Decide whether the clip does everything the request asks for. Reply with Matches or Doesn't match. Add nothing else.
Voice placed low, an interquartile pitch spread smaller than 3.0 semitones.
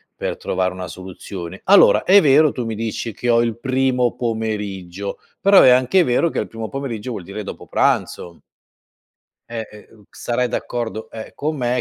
Doesn't match